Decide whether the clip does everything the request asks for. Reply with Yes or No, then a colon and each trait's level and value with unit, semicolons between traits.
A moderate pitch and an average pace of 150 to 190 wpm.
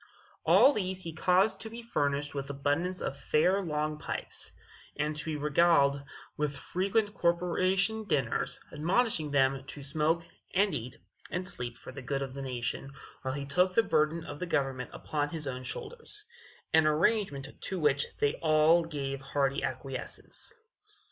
Yes: medium, 150 Hz; average, 155 wpm